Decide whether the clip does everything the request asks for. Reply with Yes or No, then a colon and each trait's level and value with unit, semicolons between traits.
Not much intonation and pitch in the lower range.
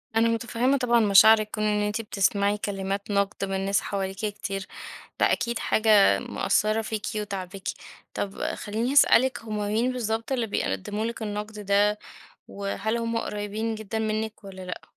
No: narrow, 2.0 semitones; high, 210 Hz